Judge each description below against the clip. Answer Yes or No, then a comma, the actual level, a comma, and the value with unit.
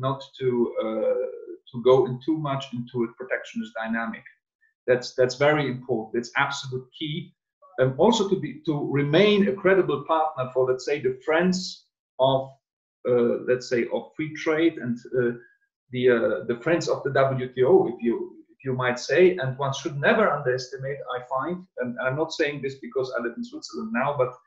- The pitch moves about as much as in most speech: No, wide, 6.5 semitones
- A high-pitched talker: No, medium, 140 Hz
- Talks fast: No, average, 185 wpm